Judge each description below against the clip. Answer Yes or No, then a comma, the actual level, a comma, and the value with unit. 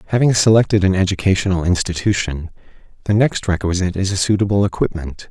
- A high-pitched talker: No, very low, 95 Hz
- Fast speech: No, slow, 135 wpm